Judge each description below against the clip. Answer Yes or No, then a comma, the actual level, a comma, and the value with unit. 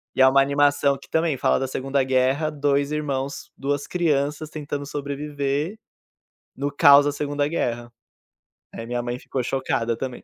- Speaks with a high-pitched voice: No, medium, 140 Hz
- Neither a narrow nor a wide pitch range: No, narrow, 1.6 semitones